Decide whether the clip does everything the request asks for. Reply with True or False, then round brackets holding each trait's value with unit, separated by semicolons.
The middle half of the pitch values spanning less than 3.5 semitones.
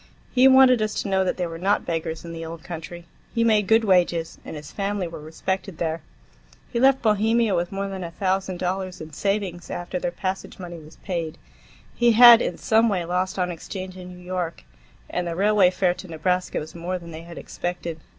True (2.9 semitones)